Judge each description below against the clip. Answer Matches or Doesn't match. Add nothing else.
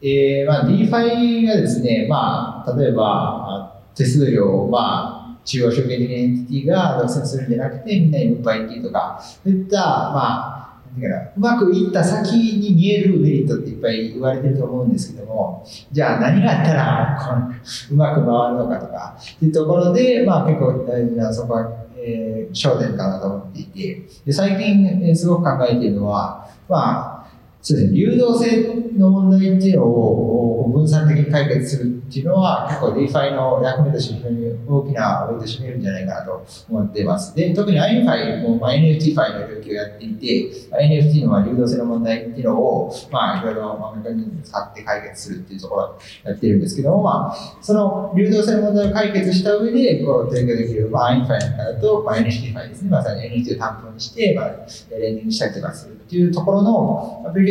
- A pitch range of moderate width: Doesn't match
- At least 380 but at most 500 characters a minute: Matches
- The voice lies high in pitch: Doesn't match